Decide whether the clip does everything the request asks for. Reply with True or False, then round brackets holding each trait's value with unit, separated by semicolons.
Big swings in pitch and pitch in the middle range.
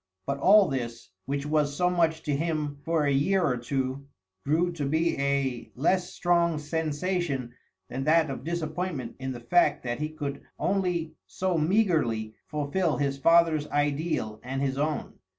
False (3.6 semitones; 150 Hz)